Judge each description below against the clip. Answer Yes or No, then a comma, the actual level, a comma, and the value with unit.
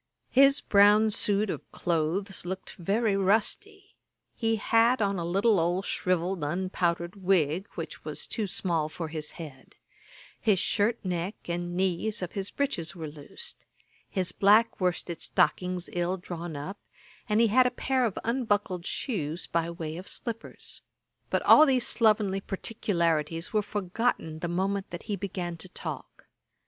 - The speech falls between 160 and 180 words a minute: No, average, 150 wpm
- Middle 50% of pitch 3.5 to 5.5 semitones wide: Yes, average, 3.8 semitones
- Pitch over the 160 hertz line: Yes, high, 190 Hz